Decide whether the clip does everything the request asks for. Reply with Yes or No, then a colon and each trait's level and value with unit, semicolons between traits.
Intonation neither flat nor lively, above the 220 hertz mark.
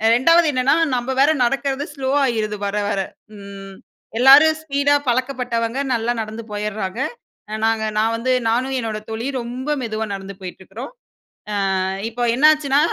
Yes: average, 4.0 semitones; high, 240 Hz